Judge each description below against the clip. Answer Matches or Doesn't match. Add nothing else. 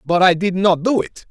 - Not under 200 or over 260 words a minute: Doesn't match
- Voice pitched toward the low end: Doesn't match